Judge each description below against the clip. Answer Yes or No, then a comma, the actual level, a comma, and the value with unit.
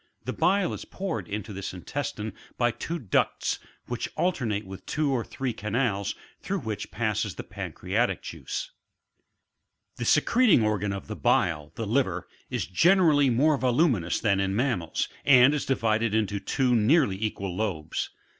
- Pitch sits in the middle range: No, low, 115 Hz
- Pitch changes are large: Yes, wide, 6.0 semitones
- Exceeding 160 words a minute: No, average, 155 wpm